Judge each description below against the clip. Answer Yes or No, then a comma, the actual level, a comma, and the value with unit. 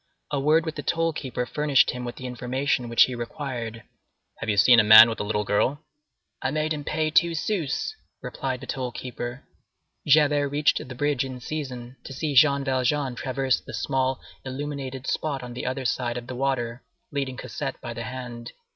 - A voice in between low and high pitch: No, low, 130 Hz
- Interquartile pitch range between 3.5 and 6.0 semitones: No, average, 3.0 semitones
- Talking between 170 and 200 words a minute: Yes, average, 190 wpm